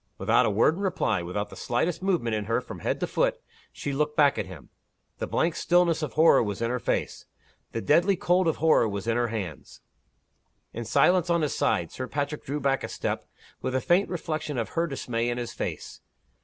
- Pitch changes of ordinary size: No, wide, 6.4 semitones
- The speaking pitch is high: No, medium, 140 Hz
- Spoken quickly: Yes, fast, 215 wpm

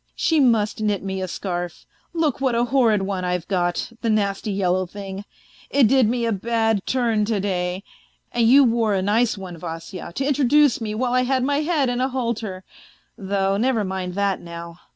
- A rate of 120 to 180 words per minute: No, average, 195 wpm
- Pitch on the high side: Yes, high, 215 Hz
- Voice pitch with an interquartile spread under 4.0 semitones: No, average, 4.4 semitones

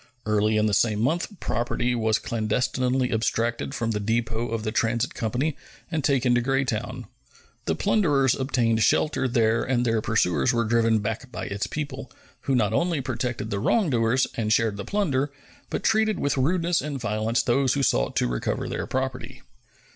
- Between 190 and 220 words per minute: No, average, 170 wpm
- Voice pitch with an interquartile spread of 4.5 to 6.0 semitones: No, average, 3.4 semitones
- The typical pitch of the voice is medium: No, low, 120 Hz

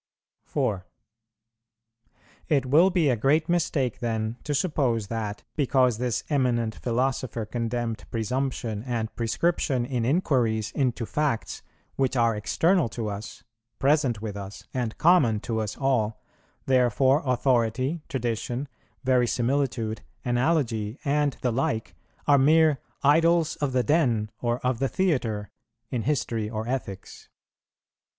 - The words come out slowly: Yes, slow, 125 wpm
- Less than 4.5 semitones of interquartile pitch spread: Yes, average, 3.9 semitones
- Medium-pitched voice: No, low, 125 Hz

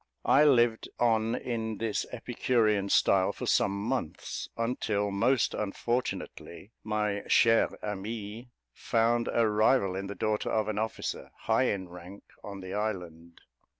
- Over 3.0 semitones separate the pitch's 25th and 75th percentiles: No, narrow, 2.6 semitones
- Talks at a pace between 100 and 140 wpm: Yes, slow, 135 wpm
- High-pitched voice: No, low, 110 Hz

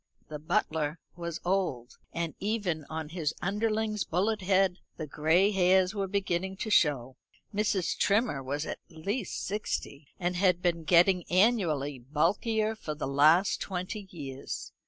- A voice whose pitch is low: No, medium, 180 Hz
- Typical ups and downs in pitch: Yes, average, 4.4 semitones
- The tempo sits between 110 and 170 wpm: Yes, average, 140 wpm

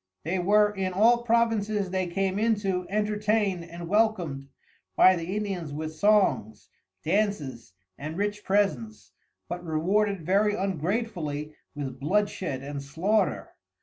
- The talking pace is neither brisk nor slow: No, slow, 120 wpm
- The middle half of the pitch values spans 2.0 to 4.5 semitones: No, average, 4.9 semitones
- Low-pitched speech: No, high, 190 Hz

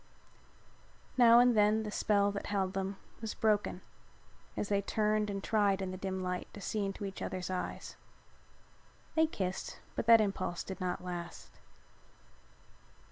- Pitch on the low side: No, high, 200 Hz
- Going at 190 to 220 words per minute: No, average, 150 wpm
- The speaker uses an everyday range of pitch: No, narrow, 2.2 semitones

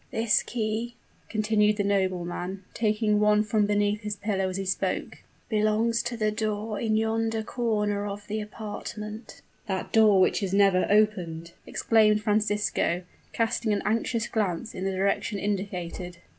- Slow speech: No, average, 145 wpm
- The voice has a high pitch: Yes, high, 210 Hz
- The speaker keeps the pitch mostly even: Yes, narrow, 1.7 semitones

